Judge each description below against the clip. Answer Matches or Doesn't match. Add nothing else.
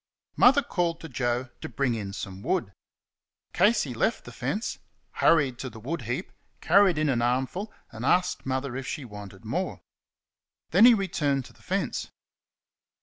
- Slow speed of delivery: Doesn't match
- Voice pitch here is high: Doesn't match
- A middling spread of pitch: Doesn't match